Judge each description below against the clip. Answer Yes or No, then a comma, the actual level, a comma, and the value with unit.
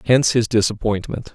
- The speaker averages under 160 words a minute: Yes, slow, 135 wpm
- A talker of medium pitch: No, low, 110 Hz